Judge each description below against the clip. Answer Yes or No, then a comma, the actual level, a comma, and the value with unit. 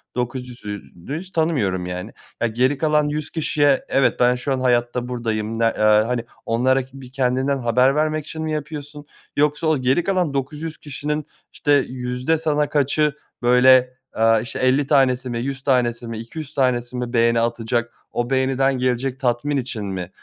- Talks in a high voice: No, low, 130 Hz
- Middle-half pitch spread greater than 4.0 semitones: No, average, 3.3 semitones